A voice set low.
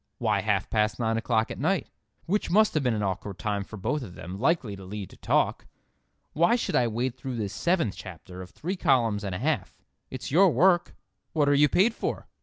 Yes: low, 115 Hz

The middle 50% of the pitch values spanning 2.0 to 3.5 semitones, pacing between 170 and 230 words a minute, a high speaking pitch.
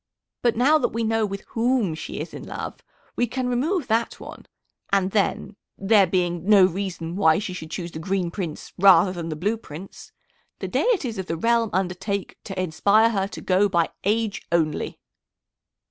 No: average, 4.2 semitones; average, 180 wpm; high, 195 Hz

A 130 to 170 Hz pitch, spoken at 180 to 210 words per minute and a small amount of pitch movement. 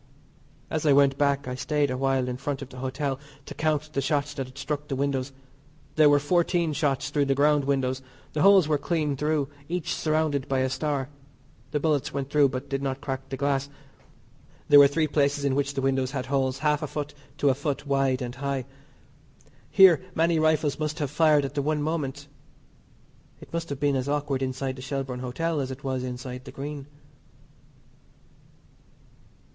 Yes: medium, 140 Hz; average, 195 wpm; narrow, 1.9 semitones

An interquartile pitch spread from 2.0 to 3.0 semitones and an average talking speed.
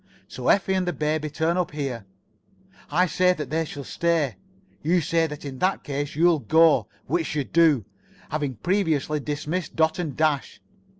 Yes: average, 2.7 semitones; average, 170 wpm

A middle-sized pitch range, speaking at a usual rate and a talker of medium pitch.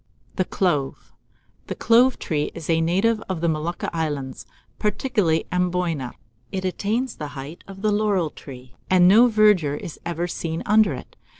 Yes: average, 4.9 semitones; average, 165 wpm; medium, 175 Hz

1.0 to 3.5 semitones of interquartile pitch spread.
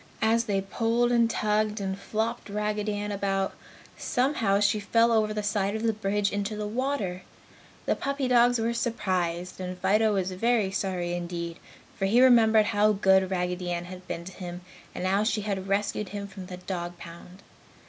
Yes: average, 2.9 semitones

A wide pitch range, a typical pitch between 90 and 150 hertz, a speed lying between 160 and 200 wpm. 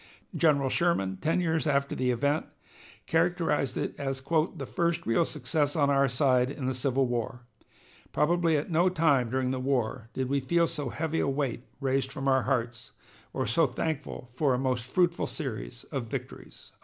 No: average, 3.9 semitones; medium, 140 Hz; average, 175 wpm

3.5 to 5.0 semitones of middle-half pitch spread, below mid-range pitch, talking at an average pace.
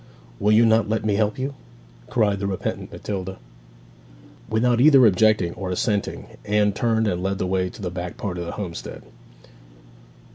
No: average, 3.0 semitones; low, 105 Hz; average, 170 wpm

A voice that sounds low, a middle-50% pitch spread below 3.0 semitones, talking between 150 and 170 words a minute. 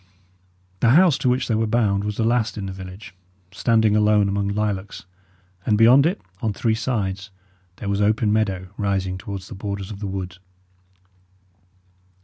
Yes: low, 105 Hz; narrow, 2.4 semitones; average, 165 wpm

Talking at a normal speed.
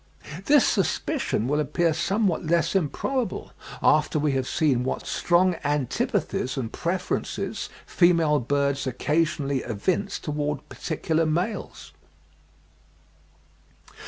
No: slow, 100 wpm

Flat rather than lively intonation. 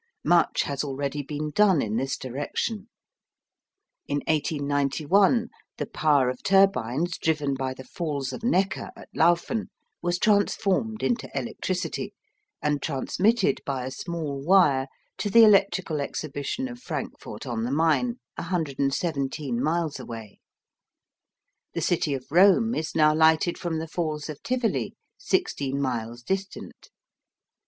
No: wide, 5.6 semitones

